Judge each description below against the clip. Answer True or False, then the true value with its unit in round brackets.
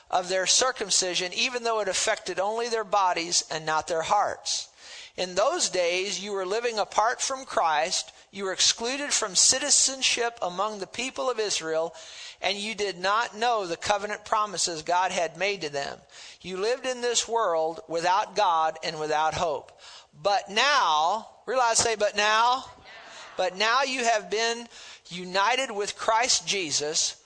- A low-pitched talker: False (205 Hz)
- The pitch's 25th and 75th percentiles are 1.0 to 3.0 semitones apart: False (4.7 semitones)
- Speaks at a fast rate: False (155 wpm)